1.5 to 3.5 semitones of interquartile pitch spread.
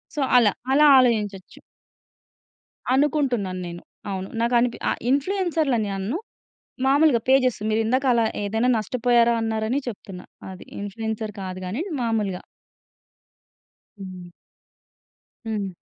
No: average, 4.2 semitones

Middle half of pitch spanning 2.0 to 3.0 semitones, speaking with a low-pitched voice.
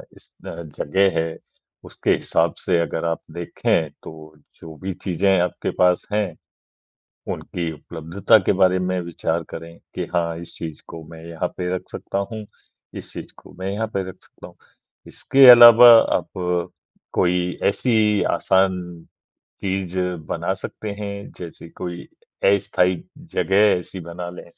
Yes: narrow, 2.6 semitones; very low, 90 Hz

